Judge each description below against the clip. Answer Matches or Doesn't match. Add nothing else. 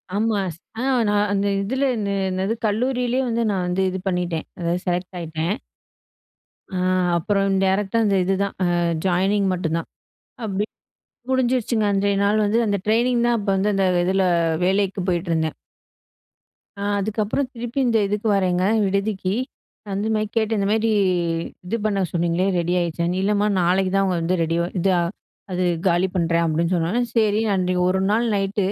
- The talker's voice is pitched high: Matches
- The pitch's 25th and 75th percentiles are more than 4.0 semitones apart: Doesn't match